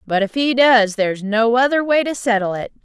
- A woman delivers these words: Yes, female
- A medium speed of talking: No, fast, 230 wpm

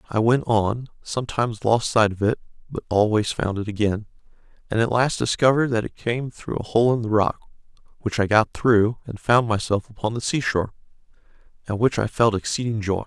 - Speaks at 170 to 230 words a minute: Yes, average, 195 wpm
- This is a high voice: No, low, 115 Hz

